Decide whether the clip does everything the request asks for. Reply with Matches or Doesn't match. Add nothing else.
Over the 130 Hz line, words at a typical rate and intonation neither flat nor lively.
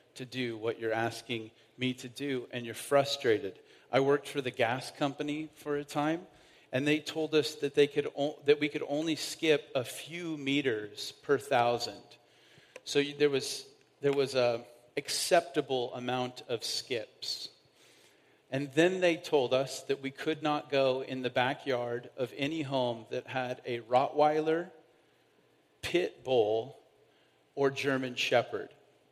Matches